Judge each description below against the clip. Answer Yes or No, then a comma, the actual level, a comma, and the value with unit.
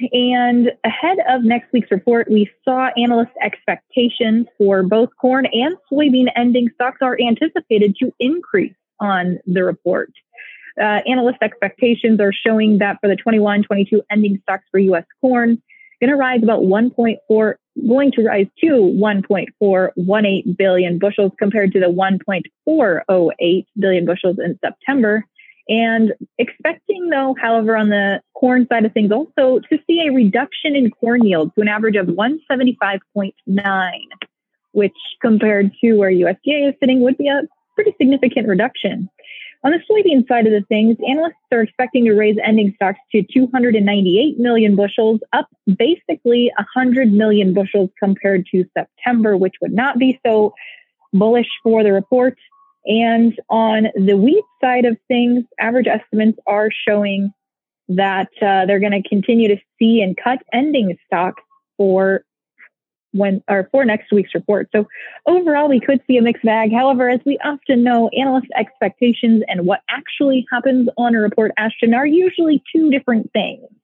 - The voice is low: No, high, 230 Hz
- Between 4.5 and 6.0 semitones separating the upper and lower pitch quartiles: No, average, 4.1 semitones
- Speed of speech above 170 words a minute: No, average, 155 wpm